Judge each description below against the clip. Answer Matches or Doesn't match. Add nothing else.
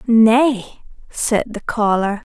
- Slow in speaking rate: Matches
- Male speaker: Doesn't match